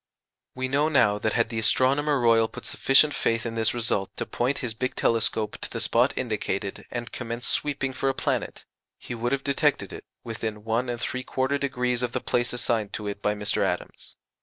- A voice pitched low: Yes, low, 120 Hz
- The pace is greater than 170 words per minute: Yes, average, 190 wpm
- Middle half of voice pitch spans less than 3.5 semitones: Yes, average, 2.8 semitones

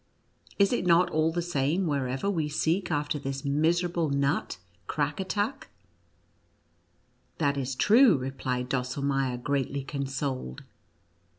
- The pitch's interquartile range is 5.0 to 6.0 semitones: No, average, 4.2 semitones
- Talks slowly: Yes, slow, 120 wpm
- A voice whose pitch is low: No, medium, 145 Hz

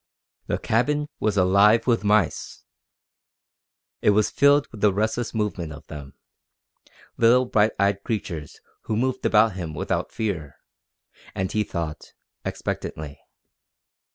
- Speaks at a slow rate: Yes, slow, 125 wpm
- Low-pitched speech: Yes, low, 105 Hz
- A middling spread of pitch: Yes, average, 3.9 semitones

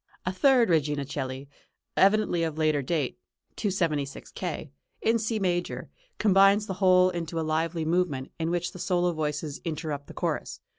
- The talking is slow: No, average, 155 wpm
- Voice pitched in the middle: Yes, medium, 170 Hz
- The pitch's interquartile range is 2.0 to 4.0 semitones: Yes, average, 3.4 semitones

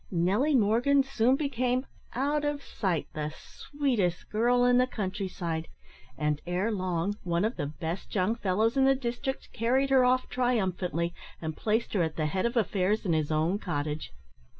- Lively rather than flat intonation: Yes, wide, 6.5 semitones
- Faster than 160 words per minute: Yes, average, 170 wpm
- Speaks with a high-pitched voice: Yes, high, 210 Hz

